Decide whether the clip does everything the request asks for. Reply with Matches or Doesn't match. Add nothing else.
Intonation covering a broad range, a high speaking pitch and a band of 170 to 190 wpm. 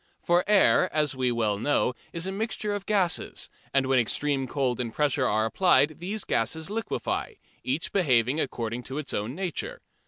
Doesn't match